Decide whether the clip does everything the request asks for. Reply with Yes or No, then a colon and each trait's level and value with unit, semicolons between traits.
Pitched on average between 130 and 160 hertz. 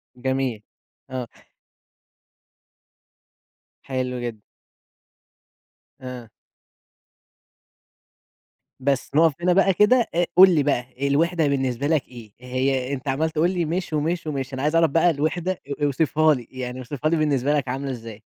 Yes: medium, 140 Hz